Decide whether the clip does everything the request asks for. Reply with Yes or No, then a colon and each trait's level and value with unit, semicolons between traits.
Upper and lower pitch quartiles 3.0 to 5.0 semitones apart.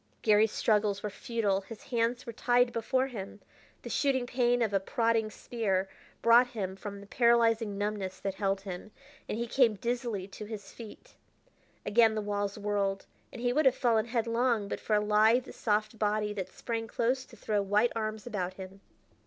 No: narrow, 2.6 semitones